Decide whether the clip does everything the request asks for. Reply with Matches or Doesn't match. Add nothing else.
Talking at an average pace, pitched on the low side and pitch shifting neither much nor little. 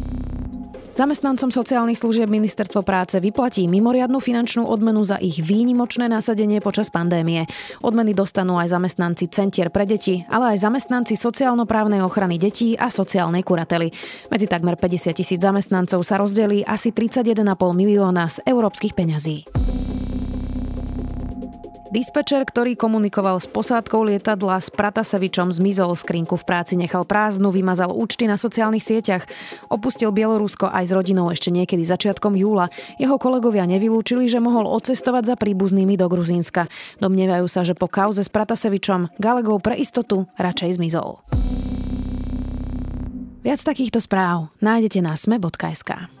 Doesn't match